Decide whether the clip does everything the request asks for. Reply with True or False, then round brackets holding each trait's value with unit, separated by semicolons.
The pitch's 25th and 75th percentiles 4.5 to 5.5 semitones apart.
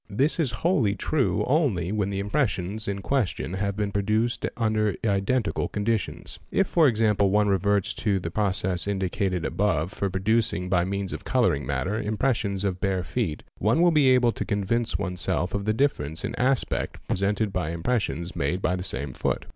False (3.5 semitones)